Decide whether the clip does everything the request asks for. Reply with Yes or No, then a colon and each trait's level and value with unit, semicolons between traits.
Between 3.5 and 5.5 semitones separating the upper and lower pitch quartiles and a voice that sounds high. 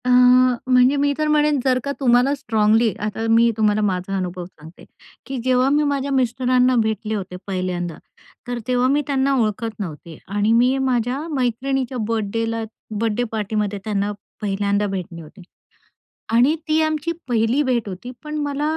Yes: average, 4.1 semitones; high, 235 Hz